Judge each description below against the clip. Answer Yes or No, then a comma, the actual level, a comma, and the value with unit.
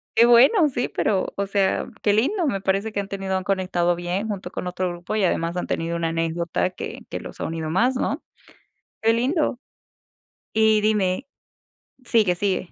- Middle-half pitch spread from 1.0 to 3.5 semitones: No, average, 4.0 semitones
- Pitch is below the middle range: No, high, 195 Hz